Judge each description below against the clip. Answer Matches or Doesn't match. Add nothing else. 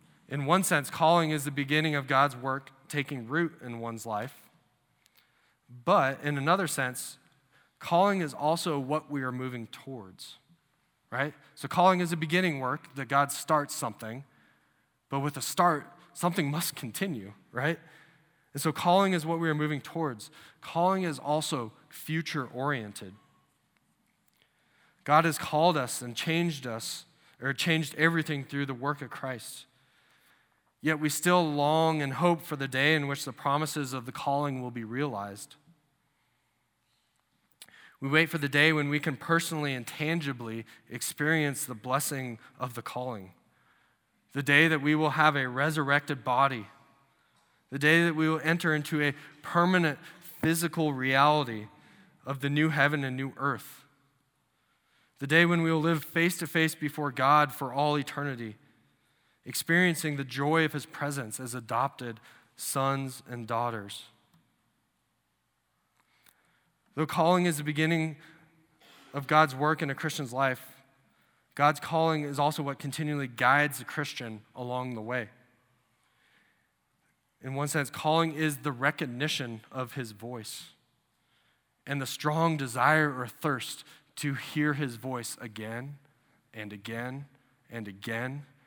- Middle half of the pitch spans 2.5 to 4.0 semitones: Matches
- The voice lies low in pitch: Doesn't match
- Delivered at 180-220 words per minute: Doesn't match